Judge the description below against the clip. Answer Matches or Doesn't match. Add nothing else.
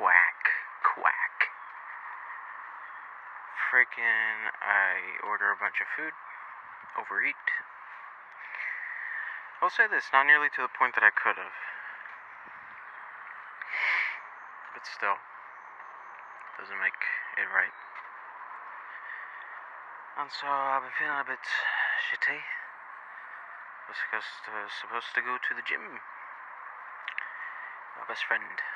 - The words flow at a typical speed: Doesn't match